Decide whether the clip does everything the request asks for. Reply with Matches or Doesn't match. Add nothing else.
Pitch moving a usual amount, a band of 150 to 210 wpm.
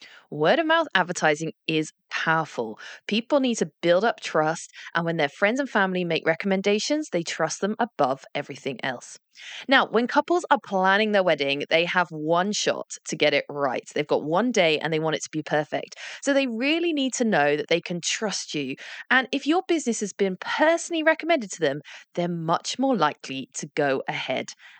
Doesn't match